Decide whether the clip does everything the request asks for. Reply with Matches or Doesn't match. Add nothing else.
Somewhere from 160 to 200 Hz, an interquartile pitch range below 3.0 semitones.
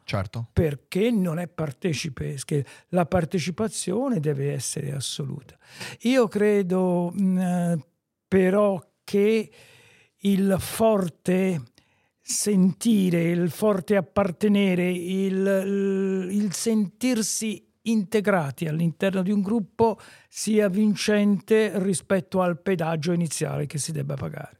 Doesn't match